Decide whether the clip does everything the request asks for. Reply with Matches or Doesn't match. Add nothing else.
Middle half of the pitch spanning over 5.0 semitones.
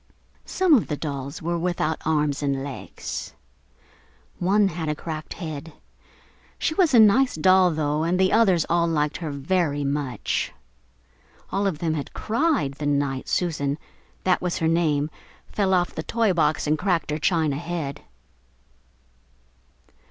Doesn't match